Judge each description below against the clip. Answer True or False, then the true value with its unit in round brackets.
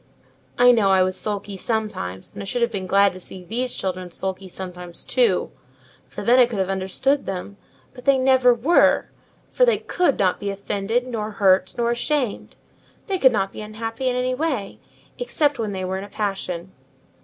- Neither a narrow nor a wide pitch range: True (4.7 semitones)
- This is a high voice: True (210 Hz)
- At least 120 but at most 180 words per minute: False (190 wpm)